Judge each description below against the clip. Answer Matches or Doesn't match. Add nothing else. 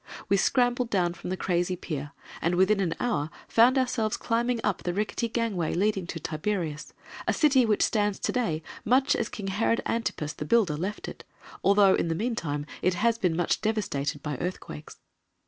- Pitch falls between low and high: Doesn't match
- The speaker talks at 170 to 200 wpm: Matches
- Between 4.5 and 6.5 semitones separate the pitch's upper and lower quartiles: Matches